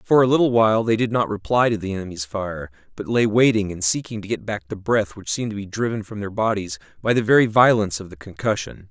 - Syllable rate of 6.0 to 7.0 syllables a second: Yes, 6.3 syllables/s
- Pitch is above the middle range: No, low, 105 Hz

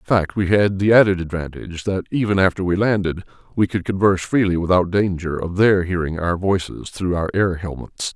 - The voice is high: No, very low, 95 Hz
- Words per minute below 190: No, average, 200 wpm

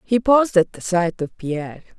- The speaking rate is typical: No, fast, 210 wpm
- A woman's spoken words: Yes, female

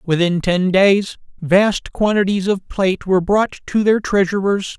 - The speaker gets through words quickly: No, average, 150 wpm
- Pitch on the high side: Yes, high, 195 Hz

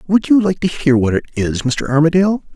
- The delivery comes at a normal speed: No, fast, 235 wpm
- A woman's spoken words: No, male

